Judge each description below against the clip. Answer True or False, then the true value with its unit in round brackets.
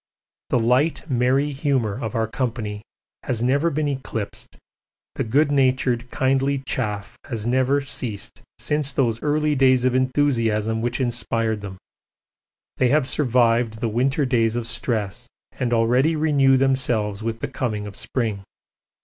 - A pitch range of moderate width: True (3.2 semitones)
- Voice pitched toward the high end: False (125 Hz)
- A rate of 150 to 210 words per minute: False (140 wpm)